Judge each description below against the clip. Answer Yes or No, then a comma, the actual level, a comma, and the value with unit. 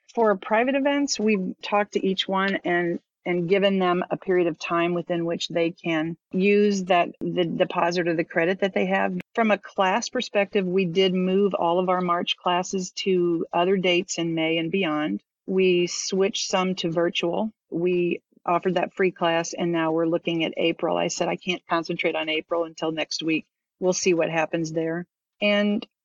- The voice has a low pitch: No, medium, 180 Hz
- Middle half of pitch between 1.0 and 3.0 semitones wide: Yes, narrow, 2.4 semitones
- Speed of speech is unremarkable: Yes, average, 185 wpm